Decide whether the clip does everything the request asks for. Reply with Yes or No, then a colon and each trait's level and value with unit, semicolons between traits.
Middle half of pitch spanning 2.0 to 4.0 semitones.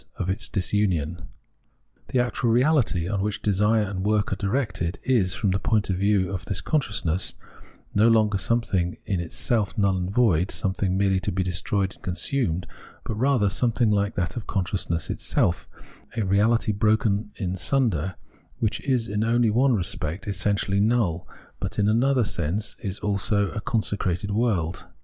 Yes: average, 3.2 semitones